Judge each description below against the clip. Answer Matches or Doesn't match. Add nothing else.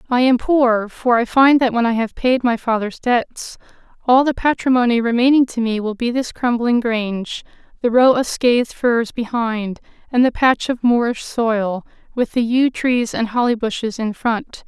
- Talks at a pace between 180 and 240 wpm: Matches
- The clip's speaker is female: Matches